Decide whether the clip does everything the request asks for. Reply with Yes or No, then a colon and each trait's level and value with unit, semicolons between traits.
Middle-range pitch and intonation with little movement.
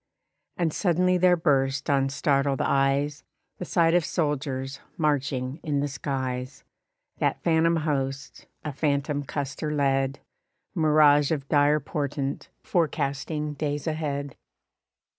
Yes: medium, 145 Hz; narrow, 2.2 semitones